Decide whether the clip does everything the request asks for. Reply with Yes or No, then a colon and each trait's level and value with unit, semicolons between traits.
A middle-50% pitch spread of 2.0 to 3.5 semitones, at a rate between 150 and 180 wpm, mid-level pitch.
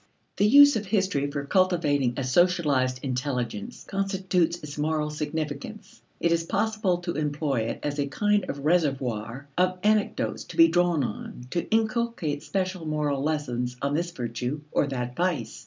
No: average, 4.9 semitones; average, 155 wpm; medium, 155 Hz